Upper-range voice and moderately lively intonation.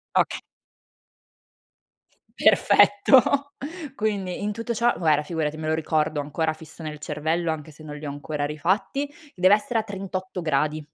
No: medium, 160 Hz; average, 5.0 semitones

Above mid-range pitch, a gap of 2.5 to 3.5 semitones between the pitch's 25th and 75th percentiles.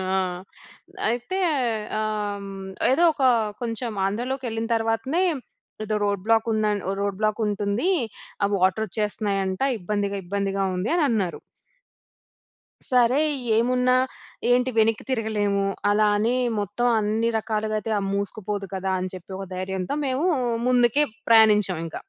Yes: high, 215 Hz; average, 2.9 semitones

